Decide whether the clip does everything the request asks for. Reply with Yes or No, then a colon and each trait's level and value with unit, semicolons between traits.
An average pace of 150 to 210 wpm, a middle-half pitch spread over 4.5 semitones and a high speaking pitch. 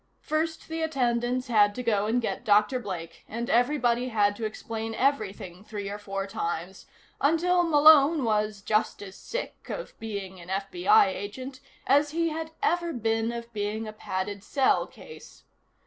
Yes: average, 160 wpm; wide, 5.6 semitones; high, 230 Hz